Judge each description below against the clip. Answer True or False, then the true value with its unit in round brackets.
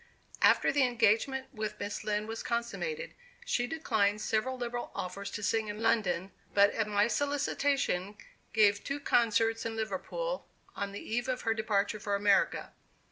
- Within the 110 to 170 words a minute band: True (155 wpm)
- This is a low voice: False (220 Hz)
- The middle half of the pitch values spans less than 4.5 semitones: True (3.1 semitones)